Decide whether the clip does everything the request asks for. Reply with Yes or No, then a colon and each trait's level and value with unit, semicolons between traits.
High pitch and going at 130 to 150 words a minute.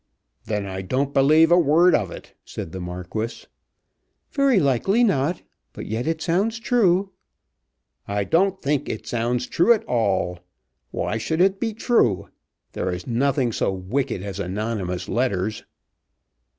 No: low, 125 Hz; average, 145 wpm